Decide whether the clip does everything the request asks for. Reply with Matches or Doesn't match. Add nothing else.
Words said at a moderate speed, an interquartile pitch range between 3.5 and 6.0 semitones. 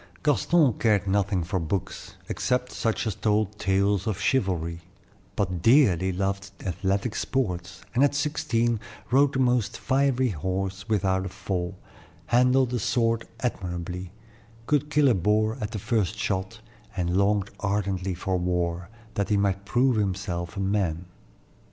Matches